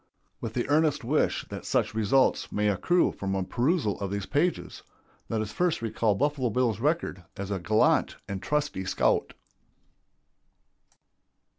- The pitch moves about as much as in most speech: No, wide, 6.5 semitones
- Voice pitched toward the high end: No, low, 115 Hz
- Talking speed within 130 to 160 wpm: Yes, average, 145 wpm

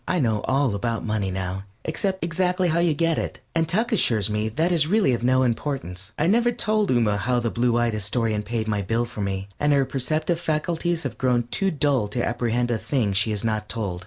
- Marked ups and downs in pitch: Yes, wide, 6.9 semitones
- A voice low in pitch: Yes, low, 120 Hz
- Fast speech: Yes, fast, 220 wpm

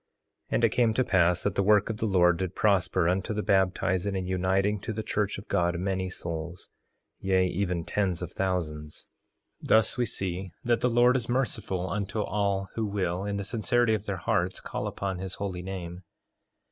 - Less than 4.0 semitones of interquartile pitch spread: Yes, narrow, 2.6 semitones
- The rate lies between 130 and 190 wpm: No, average, 200 wpm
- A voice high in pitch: No, very low, 95 Hz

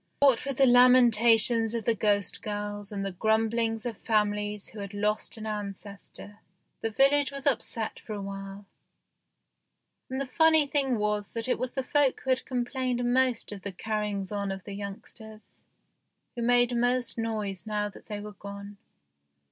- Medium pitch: No, high, 220 Hz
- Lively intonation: No, average, 3.2 semitones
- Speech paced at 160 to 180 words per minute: Yes, average, 170 wpm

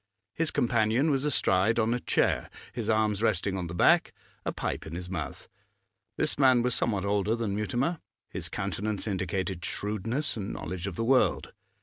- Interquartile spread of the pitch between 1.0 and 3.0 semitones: No, average, 3.9 semitones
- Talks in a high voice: No, low, 110 Hz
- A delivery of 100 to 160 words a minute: No, average, 175 wpm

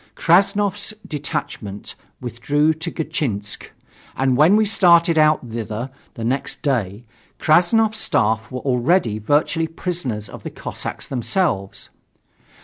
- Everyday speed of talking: No, slow, 115 wpm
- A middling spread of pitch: No, wide, 7.0 semitones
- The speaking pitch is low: No, medium, 145 Hz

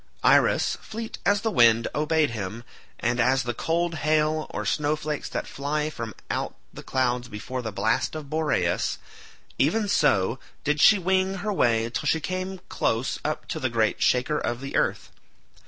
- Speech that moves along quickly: No, average, 170 wpm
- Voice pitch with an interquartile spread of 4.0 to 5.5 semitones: Yes, average, 5.2 semitones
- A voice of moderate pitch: Yes, medium, 145 Hz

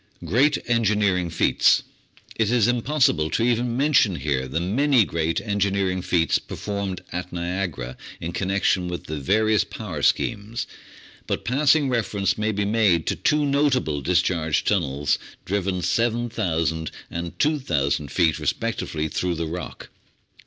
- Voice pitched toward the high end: No, very low, 95 Hz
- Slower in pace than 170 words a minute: Yes, average, 140 wpm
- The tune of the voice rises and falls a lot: Yes, wide, 5.9 semitones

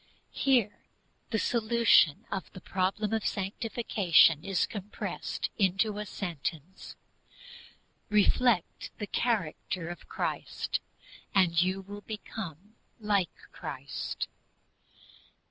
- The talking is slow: Yes, slow, 95 wpm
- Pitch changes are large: No, average, 3.2 semitones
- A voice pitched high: Yes, high, 195 Hz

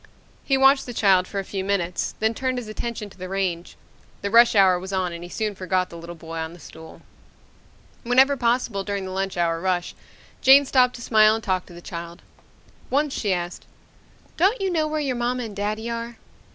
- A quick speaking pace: Yes, fast, 210 wpm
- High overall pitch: Yes, high, 205 Hz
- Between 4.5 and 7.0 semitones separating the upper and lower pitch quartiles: Yes, average, 5.1 semitones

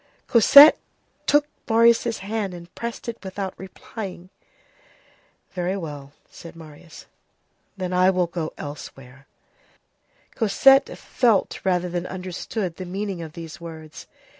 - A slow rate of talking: Yes, slow, 115 wpm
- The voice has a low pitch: No, medium, 185 Hz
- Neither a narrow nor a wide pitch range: Yes, average, 3.9 semitones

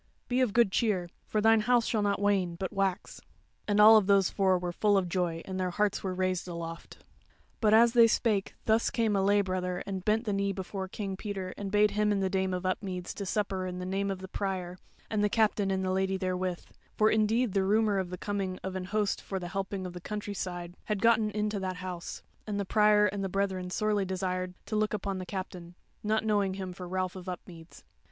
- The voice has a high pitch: Yes, high, 195 Hz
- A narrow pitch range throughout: Yes, narrow, 2.2 semitones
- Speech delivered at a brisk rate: Yes, fast, 225 wpm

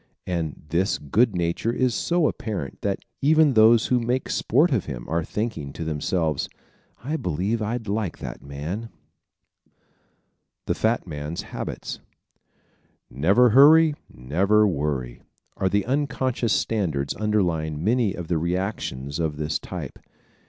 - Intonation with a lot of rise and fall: Yes, wide, 7.0 semitones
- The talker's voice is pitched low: Yes, very low, 95 Hz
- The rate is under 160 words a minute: Yes, average, 140 wpm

